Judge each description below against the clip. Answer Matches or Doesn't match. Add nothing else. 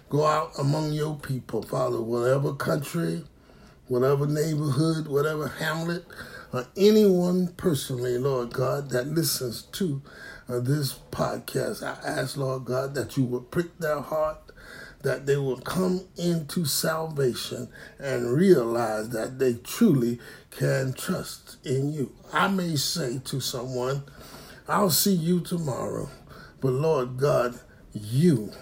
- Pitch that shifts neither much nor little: Matches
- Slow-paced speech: Matches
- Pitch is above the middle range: Doesn't match